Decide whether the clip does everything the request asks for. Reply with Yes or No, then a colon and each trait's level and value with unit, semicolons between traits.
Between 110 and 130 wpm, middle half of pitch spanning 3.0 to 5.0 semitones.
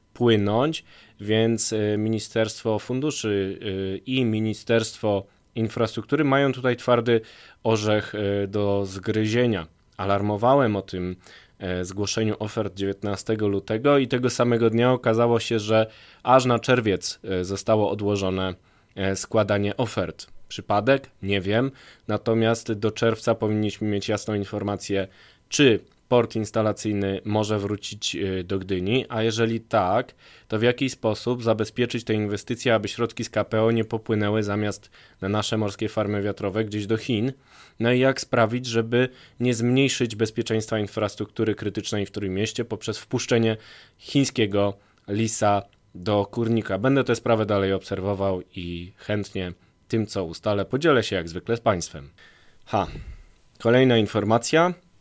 No: average, 125 wpm; narrow, 2.4 semitones